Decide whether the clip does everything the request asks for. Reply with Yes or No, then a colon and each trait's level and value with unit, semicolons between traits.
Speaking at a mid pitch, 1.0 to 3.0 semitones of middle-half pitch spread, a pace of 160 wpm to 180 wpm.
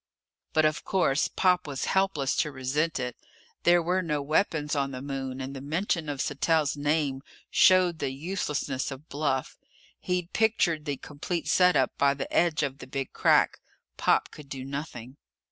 No: medium, 145 Hz; average, 3.5 semitones; average, 170 wpm